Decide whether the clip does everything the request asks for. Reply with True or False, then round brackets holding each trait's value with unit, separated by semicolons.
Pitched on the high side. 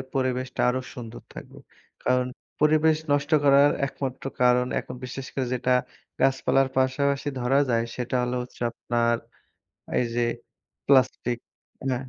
False (130 Hz)